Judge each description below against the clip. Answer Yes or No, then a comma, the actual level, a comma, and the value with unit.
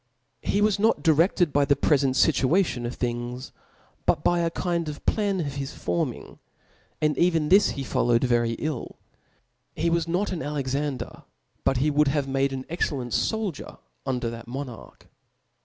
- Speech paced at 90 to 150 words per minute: No, average, 160 wpm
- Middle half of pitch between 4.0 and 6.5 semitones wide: Yes, average, 4.6 semitones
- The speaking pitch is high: No, medium, 145 Hz